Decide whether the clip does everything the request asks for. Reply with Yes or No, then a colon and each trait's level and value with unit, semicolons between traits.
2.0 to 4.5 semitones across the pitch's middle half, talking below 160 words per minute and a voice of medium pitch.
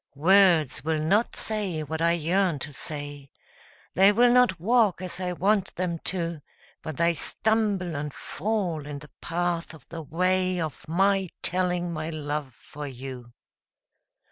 Yes: average, 3.7 semitones; average, 150 wpm; medium, 170 Hz